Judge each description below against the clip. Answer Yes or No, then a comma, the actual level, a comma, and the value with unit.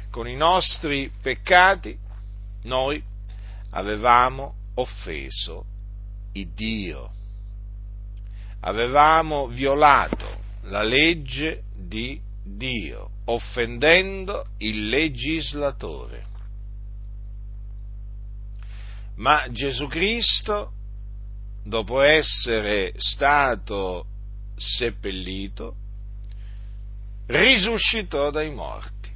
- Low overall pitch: Yes, low, 100 Hz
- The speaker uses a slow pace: Yes, slow, 60 wpm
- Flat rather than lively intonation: No, average, 4.8 semitones